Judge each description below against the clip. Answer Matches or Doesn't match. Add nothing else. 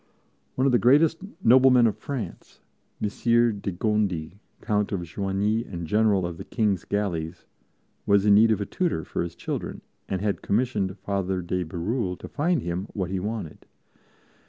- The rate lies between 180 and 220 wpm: Doesn't match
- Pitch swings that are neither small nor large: Matches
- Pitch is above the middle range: Doesn't match